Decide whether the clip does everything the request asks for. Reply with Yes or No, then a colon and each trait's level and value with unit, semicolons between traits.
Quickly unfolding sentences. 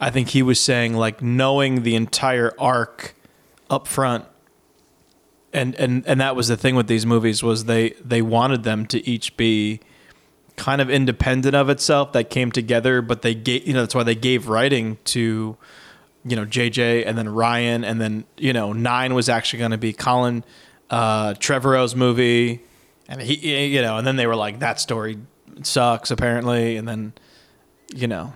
No: average, 180 wpm